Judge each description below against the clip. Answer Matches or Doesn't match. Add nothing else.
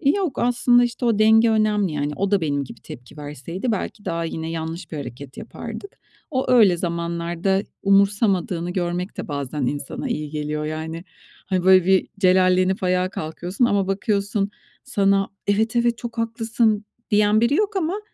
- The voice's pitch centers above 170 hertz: Matches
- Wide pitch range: Doesn't match